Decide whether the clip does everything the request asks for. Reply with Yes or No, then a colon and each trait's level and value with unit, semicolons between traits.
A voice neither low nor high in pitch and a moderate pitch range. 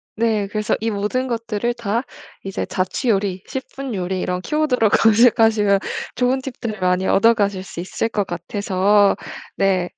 No: high, 210 Hz; average, 3.2 semitones